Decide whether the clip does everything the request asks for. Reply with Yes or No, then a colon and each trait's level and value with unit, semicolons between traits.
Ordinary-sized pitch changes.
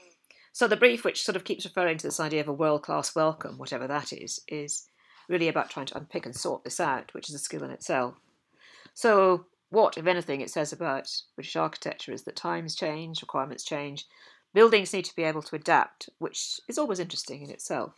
Yes: average, 4.1 semitones